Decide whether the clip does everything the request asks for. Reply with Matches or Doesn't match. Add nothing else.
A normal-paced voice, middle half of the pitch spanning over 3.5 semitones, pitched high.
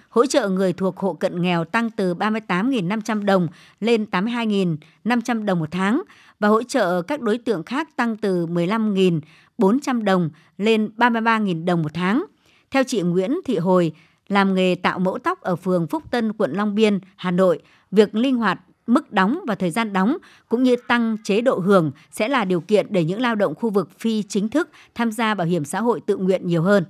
Matches